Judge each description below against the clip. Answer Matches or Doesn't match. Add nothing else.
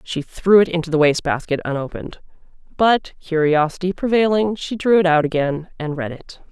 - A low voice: Doesn't match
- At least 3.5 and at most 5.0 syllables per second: Doesn't match